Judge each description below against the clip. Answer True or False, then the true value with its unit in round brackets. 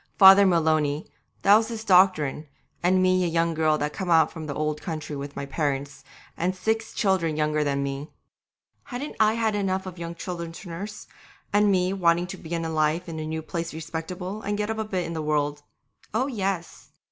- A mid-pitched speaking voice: True (170 Hz)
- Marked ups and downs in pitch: False (3.8 semitones)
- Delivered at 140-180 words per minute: False (200 wpm)